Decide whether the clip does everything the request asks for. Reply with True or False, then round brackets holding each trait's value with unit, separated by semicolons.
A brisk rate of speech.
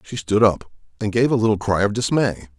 True (230 wpm)